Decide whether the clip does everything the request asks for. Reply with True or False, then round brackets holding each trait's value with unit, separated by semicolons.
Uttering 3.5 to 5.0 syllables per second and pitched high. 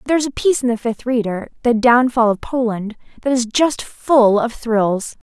True (4.9 syllables/s; 240 Hz)